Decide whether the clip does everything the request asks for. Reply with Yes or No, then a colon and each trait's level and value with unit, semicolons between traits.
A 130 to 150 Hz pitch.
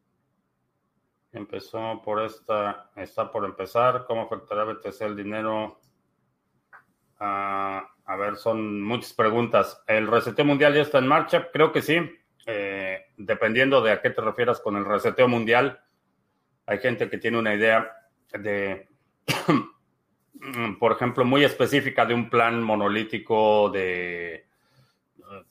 No: low, 110 Hz